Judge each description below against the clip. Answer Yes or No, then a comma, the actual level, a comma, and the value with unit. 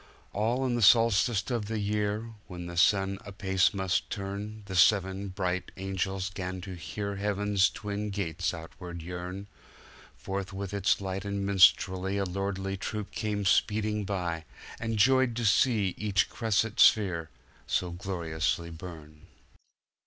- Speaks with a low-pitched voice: Yes, low, 100 Hz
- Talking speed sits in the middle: No, slow, 130 wpm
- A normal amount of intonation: No, narrow, 2.2 semitones